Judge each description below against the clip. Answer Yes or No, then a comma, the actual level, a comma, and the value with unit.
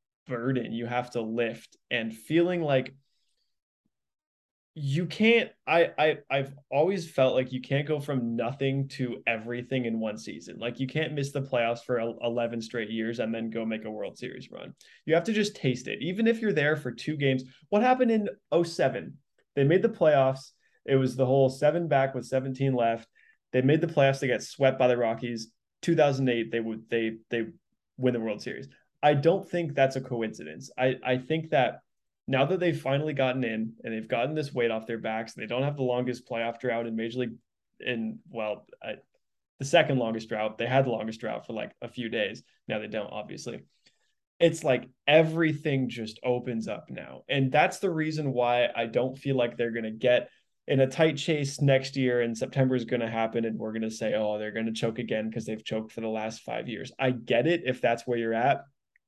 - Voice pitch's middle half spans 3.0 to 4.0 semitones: Yes, average, 3.4 semitones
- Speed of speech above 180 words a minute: Yes, fast, 205 wpm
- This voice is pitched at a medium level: No, low, 125 Hz